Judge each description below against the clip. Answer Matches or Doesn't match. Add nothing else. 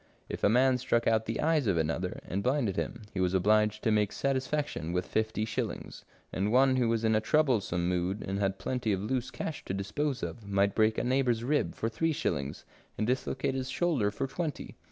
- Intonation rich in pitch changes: Doesn't match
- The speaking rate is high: Matches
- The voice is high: Doesn't match